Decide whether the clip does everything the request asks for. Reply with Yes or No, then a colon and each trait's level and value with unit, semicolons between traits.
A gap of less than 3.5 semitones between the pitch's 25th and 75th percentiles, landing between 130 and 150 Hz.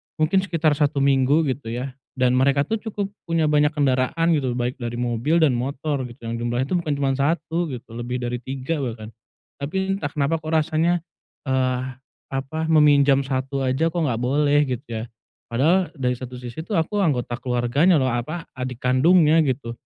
No: average, 4.0 semitones; medium, 140 Hz